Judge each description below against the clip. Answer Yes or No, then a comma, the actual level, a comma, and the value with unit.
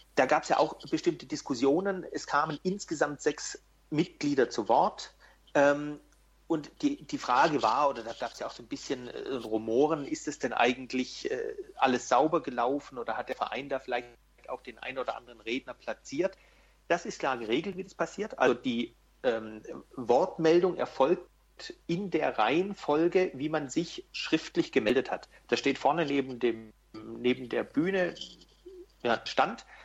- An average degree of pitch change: No, wide, 6.6 semitones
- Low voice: No, medium, 155 Hz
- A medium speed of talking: Yes, average, 165 wpm